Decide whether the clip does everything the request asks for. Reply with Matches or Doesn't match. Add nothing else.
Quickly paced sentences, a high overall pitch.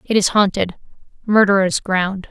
Doesn't match